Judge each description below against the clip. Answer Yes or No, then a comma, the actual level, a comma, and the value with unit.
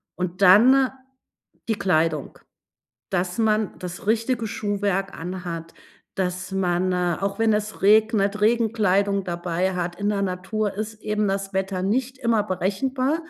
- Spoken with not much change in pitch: No, average, 3.0 semitones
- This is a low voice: No, high, 200 Hz